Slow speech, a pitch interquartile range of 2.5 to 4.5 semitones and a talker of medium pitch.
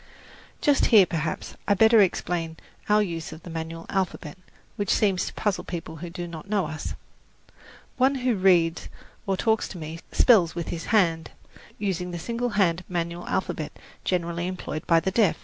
No: average, 175 wpm; average, 3.6 semitones; medium, 180 Hz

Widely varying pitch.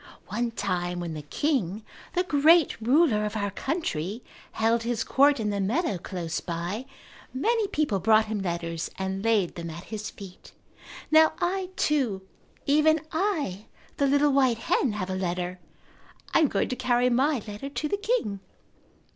Yes: wide, 7.4 semitones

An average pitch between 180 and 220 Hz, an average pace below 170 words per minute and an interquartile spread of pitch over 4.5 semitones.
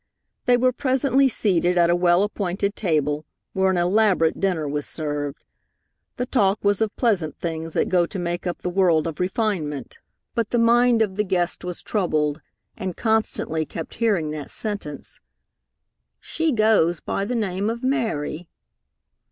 Yes: medium, 185 Hz; average, 160 wpm; average, 5.2 semitones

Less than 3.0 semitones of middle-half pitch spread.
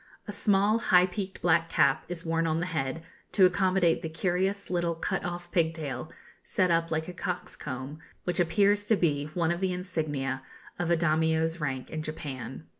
Yes: narrow, 2.4 semitones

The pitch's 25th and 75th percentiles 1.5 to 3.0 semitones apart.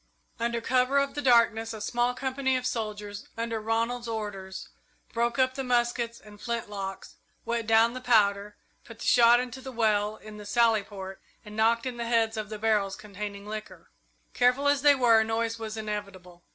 Yes: narrow, 2.5 semitones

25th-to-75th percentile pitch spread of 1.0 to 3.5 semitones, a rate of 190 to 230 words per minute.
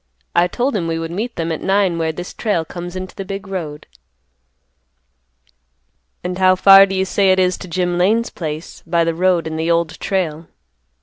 Yes: narrow, 2.6 semitones; average, 195 wpm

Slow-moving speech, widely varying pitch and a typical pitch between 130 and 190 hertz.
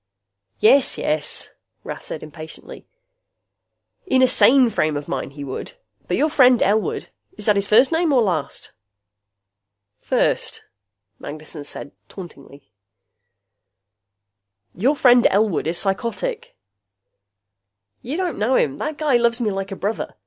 No: slow, 130 wpm; wide, 8.3 semitones; high, 215 Hz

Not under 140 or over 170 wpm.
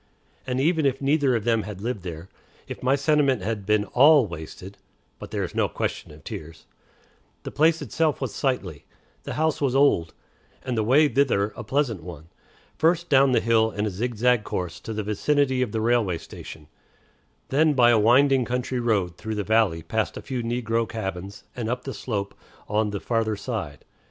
No: average, 190 wpm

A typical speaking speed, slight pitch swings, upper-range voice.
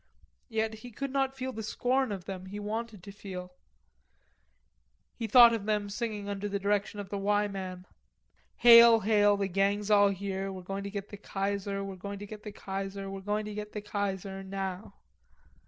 Yes: average, 190 wpm; narrow, 1.6 semitones; high, 205 Hz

